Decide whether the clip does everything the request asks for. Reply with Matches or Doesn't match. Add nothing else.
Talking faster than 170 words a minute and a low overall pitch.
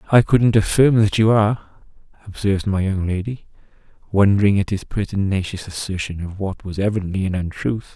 Doesn't match